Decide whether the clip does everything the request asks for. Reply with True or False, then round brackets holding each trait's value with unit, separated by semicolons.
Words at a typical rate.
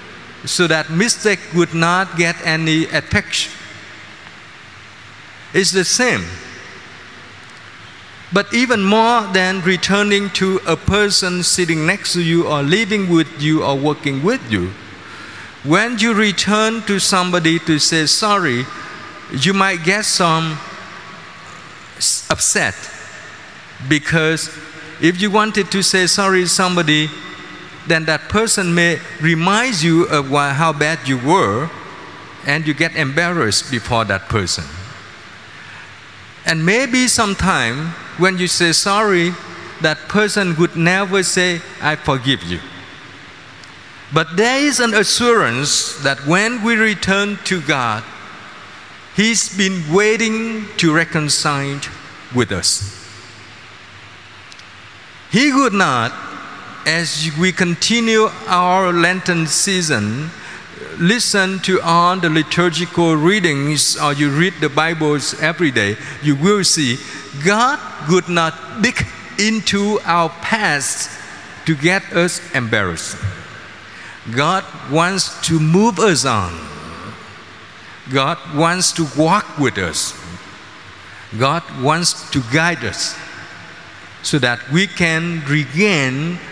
False (115 wpm)